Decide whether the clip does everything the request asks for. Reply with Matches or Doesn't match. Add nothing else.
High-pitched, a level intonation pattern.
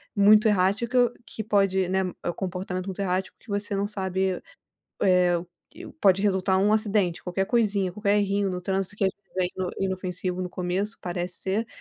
Matches